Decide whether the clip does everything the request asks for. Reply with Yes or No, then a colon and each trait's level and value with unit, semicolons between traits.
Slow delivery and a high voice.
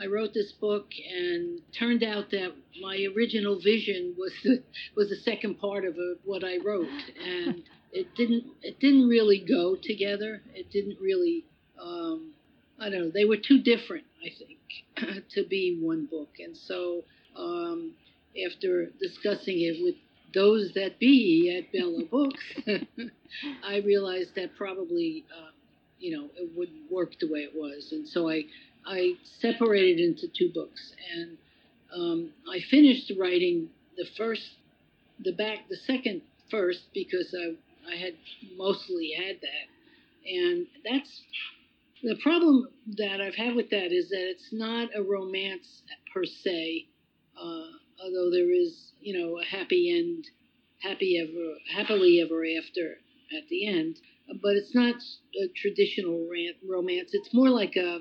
No: average, 150 wpm; high, 235 Hz